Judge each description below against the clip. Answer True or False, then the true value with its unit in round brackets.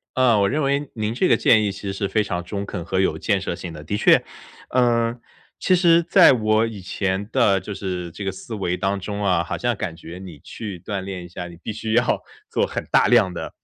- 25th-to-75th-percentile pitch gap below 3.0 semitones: False (3.8 semitones)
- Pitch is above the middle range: False (100 Hz)